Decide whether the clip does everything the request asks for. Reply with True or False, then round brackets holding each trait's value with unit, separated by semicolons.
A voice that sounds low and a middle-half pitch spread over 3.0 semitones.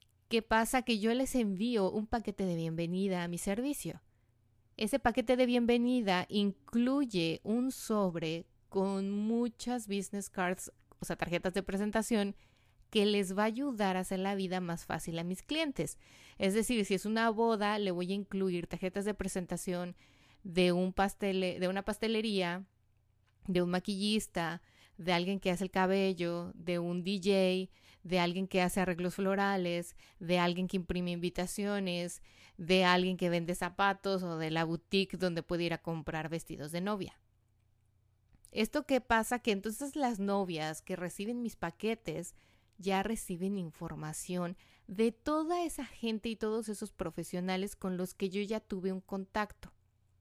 False (190 Hz; 3.4 semitones)